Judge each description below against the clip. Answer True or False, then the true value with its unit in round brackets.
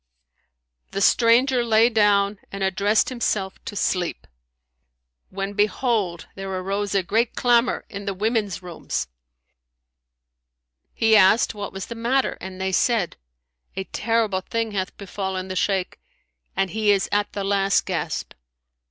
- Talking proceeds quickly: False (135 wpm)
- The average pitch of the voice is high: True (200 Hz)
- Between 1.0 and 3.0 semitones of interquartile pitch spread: True (2.7 semitones)